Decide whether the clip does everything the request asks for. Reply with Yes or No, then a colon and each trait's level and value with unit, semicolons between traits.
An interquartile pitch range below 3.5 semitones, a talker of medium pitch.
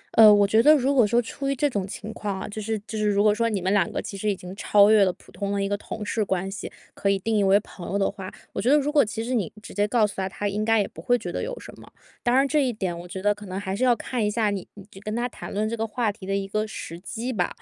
No: average, 2.7 semitones; high, 210 Hz